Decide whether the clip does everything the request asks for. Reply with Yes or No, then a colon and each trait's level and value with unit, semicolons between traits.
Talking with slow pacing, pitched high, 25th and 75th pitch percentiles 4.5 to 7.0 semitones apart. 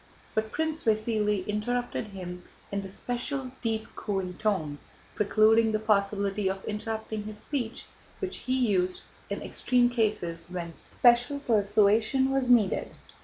No: slow, 130 wpm; high, 215 Hz; average, 3.4 semitones